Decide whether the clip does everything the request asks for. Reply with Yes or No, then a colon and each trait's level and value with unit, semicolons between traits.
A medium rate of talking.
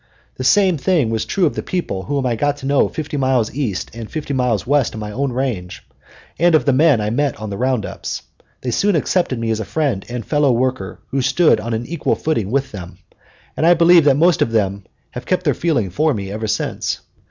No: fast, 230 wpm